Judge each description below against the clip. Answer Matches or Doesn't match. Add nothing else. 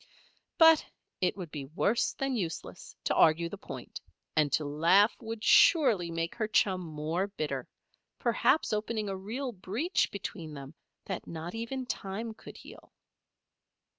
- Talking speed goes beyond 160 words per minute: Doesn't match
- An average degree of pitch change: Doesn't match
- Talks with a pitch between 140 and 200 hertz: Matches